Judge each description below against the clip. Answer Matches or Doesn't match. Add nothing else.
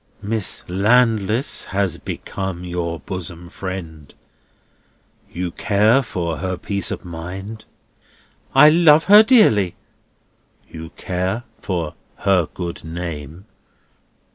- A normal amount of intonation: Matches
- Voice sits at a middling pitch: Doesn't match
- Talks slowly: Matches